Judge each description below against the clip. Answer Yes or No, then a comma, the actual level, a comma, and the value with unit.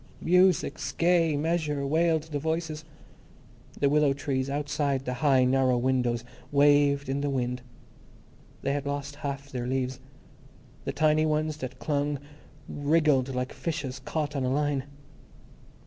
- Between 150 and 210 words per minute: No, slow, 135 wpm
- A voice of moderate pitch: Yes, medium, 145 Hz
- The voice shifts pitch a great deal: No, narrow, 2.5 semitones